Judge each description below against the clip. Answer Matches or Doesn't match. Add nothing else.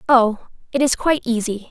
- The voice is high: Matches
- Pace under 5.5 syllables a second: Doesn't match